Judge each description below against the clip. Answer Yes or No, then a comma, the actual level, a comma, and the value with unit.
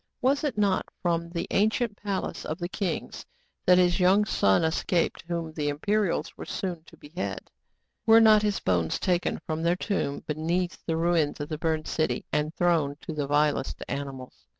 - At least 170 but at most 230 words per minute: Yes, average, 175 wpm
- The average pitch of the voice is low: No, medium, 170 Hz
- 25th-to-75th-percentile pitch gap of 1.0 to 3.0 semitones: No, average, 4.0 semitones